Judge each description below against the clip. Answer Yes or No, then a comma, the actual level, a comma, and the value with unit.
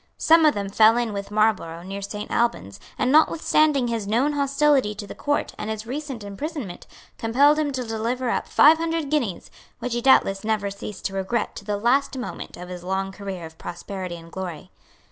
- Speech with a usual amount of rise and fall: No, wide, 5.9 semitones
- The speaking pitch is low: No, high, 220 Hz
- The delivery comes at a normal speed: Yes, average, 195 wpm